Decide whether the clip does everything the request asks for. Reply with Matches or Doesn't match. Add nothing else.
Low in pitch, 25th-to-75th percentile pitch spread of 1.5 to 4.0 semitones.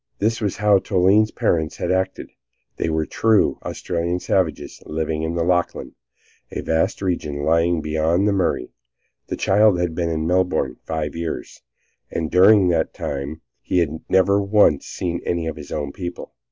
Matches